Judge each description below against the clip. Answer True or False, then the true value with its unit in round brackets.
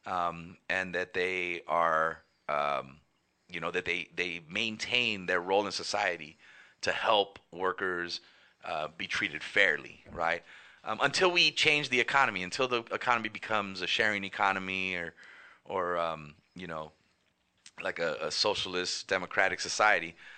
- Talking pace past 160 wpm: False (140 wpm)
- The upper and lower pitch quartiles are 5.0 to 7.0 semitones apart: False (4.2 semitones)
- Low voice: True (95 Hz)